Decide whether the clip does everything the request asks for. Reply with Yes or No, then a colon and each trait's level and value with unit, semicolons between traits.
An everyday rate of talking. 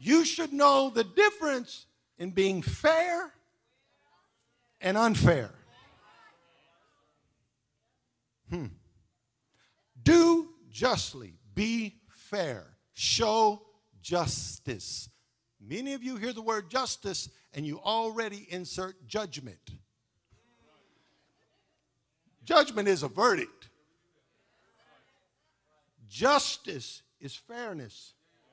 No: slow, 75 wpm